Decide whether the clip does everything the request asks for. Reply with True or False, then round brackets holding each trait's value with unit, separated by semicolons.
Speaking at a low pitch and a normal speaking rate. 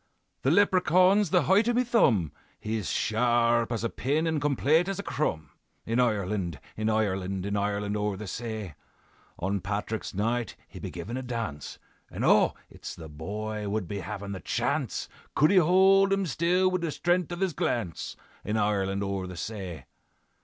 True (110 Hz; 175 wpm)